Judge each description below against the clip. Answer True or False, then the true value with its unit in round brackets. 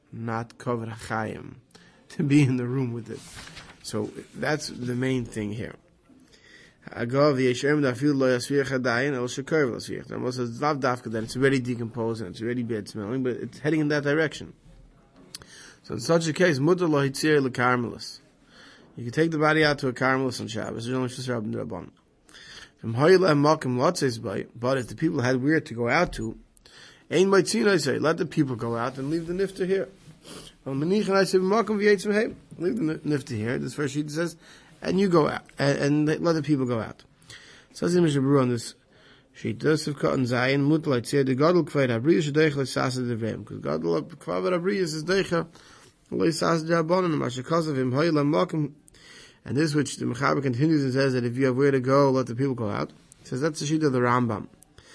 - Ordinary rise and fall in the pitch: True (4.2 semitones)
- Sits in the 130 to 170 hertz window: True (140 Hz)